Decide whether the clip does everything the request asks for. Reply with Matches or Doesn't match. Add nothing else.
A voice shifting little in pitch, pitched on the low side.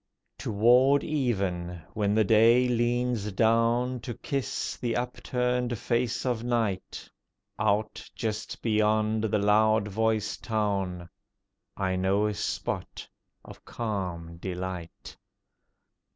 Doesn't match